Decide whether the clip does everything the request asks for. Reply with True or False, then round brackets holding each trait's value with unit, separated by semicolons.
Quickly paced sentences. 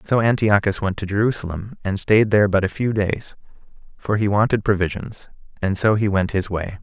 False (195 wpm)